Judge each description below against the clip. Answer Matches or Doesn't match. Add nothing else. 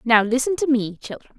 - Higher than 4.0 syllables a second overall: Matches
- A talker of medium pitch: Doesn't match